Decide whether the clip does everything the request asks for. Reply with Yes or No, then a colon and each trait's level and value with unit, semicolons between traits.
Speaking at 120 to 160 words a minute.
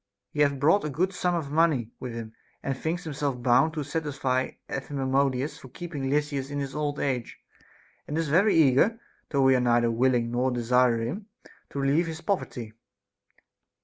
No: average, 175 wpm